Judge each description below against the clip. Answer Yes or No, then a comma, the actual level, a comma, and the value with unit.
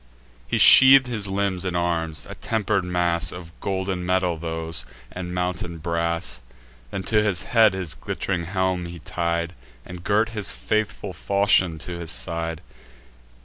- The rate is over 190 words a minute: No, average, 145 wpm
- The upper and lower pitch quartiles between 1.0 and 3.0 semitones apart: Yes, average, 2.7 semitones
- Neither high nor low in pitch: No, very low, 90 Hz